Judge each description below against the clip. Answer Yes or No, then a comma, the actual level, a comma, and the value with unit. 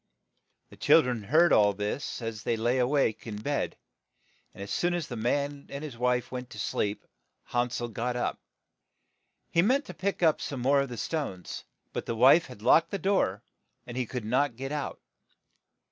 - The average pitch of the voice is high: No, low, 125 Hz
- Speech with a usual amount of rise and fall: Yes, average, 4.1 semitones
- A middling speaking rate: No, fast, 210 wpm